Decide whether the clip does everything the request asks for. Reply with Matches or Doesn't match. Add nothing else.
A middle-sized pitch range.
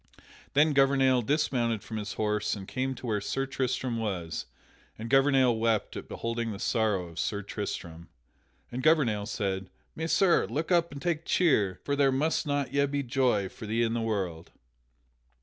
Matches